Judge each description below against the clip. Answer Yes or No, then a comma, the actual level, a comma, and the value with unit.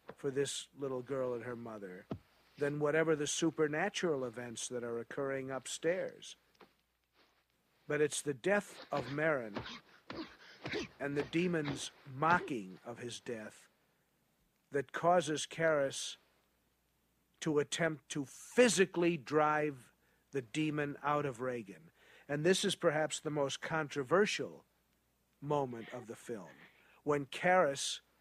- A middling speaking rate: No, slow, 115 wpm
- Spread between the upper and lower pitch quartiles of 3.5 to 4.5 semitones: No, average, 3.1 semitones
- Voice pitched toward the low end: No, medium, 145 Hz